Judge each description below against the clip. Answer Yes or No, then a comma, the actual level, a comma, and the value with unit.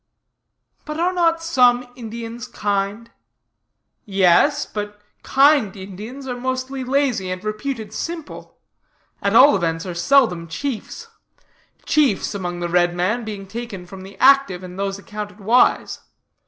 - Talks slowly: Yes, slow, 130 wpm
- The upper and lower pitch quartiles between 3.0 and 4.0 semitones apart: No, wide, 5.4 semitones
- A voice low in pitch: No, high, 215 Hz